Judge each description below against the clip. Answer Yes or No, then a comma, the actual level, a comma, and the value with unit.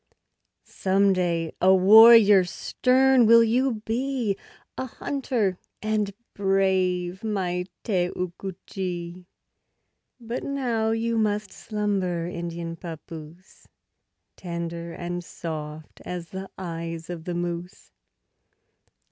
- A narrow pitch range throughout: No, average, 4.2 semitones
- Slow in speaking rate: Yes, slow, 105 wpm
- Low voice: No, high, 190 Hz